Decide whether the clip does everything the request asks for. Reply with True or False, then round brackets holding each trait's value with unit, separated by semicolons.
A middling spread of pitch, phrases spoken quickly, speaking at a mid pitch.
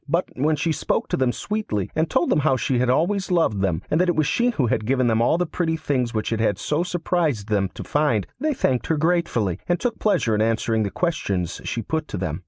False (7.3 semitones; 250 wpm; 145 Hz)